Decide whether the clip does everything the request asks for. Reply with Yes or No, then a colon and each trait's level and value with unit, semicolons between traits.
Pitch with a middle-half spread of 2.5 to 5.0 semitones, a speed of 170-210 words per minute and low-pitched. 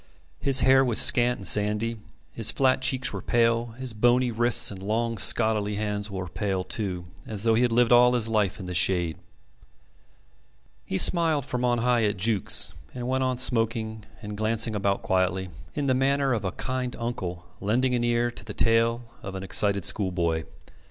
Yes: average, 3.4 semitones; average, 185 wpm; low, 115 Hz